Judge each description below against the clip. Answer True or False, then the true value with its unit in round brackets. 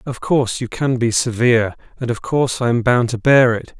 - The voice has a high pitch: False (120 Hz)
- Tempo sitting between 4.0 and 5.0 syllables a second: False (5.6 syllables/s)